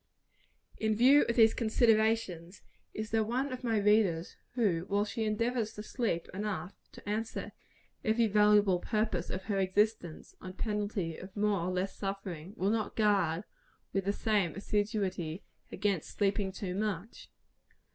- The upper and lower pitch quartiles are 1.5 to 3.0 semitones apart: Yes, average, 2.7 semitones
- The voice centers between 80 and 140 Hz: No, high, 205 Hz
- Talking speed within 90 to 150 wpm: Yes, average, 145 wpm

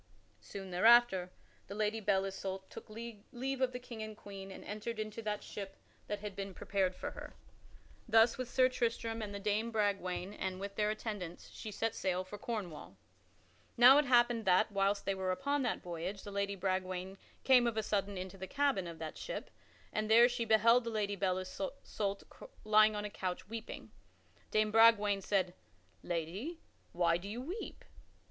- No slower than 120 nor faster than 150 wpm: No, average, 180 wpm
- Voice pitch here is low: No, high, 210 Hz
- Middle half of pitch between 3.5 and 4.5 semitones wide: No, average, 3.1 semitones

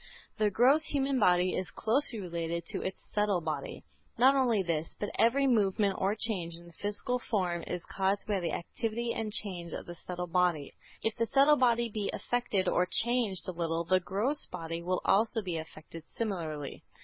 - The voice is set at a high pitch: Yes, high, 195 Hz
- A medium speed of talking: Yes, average, 185 wpm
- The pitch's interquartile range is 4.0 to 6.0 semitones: Yes, average, 4.9 semitones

